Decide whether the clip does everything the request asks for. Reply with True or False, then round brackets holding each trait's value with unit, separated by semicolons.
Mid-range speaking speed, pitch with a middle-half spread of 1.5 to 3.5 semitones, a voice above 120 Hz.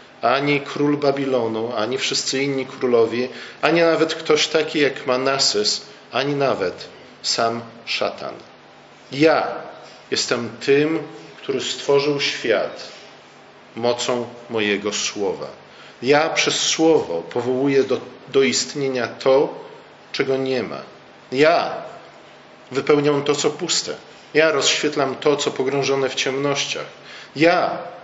False (105 wpm; 2.8 semitones; 135 Hz)